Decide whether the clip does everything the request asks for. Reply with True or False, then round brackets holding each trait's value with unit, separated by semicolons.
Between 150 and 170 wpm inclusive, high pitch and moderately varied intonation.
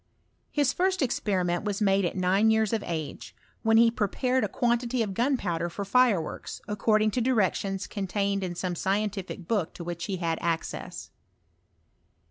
True (155 wpm; 200 Hz; 3.9 semitones)